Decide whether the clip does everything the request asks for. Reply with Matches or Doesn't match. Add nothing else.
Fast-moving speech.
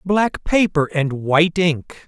Doesn't match